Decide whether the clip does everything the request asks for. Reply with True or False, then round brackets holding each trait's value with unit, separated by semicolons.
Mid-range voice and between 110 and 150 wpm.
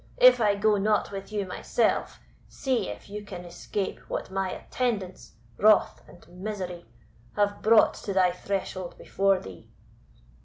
False (200 Hz; 145 wpm)